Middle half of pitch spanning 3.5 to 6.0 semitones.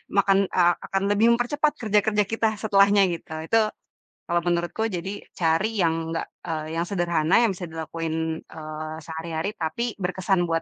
Yes: average, 4.1 semitones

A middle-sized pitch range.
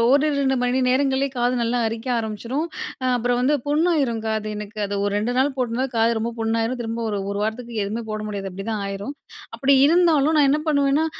Yes: average, 3.9 semitones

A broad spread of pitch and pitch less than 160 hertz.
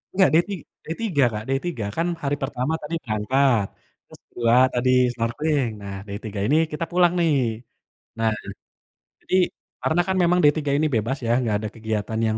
Yes: wide, 6.2 semitones; low, 135 Hz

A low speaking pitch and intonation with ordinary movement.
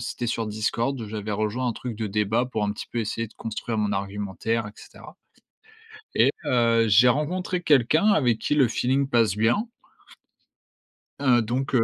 Yes: low, 115 Hz; average, 3.1 semitones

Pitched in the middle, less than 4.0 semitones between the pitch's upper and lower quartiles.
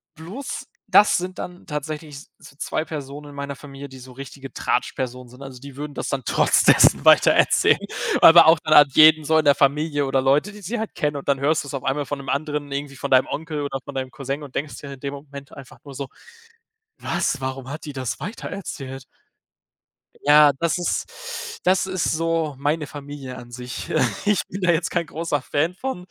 Yes: medium, 145 Hz; average, 2.9 semitones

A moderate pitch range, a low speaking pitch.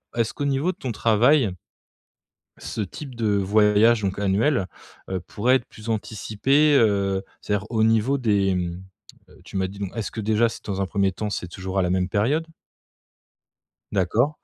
Yes: average, 3.4 semitones; low, 105 Hz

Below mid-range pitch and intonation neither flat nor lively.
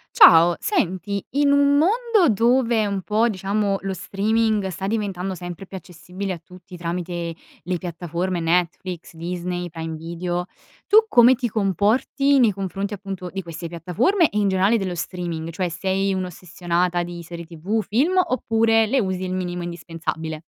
No: medium, 185 Hz; average, 3.8 semitones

